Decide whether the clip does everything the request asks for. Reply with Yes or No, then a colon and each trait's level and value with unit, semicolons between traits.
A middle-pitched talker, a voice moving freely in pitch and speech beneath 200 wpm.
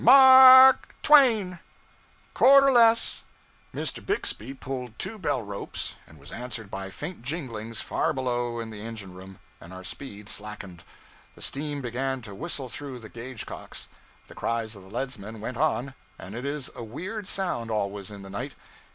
No: low, 120 Hz; wide, 6.4 semitones; average, 175 wpm